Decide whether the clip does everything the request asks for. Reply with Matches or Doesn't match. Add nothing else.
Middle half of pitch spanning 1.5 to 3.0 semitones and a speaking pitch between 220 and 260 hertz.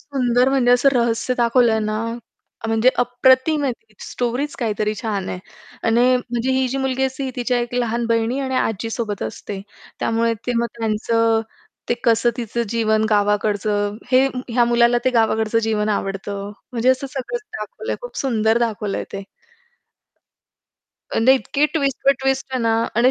Matches